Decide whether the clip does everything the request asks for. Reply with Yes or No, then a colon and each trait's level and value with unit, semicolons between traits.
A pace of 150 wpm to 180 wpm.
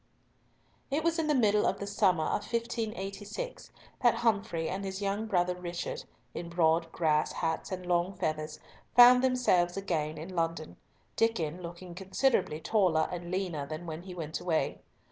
Yes: average, 160 wpm